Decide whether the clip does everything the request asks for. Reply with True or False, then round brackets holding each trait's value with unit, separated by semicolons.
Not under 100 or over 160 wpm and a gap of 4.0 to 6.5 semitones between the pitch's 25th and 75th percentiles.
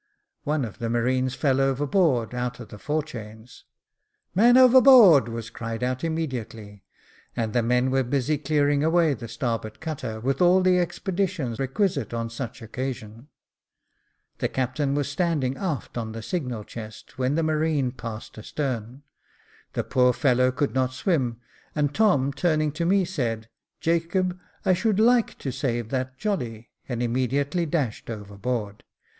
True (150 wpm; 5.2 semitones)